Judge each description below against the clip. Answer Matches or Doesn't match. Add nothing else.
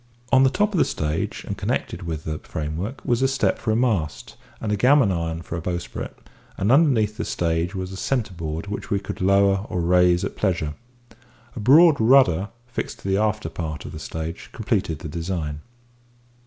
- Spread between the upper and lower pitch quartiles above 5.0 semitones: Matches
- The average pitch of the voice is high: Doesn't match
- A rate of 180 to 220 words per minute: Matches